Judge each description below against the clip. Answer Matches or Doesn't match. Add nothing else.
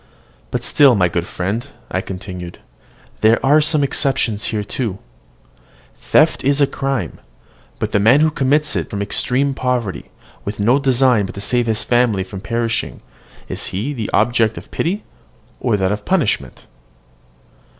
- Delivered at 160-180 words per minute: Doesn't match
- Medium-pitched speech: Doesn't match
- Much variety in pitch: Doesn't match